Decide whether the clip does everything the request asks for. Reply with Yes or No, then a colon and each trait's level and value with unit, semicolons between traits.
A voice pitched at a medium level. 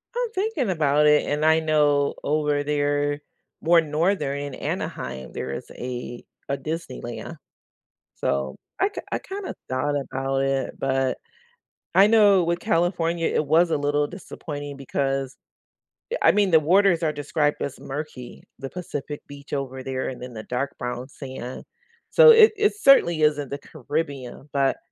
Yes: medium, 145 Hz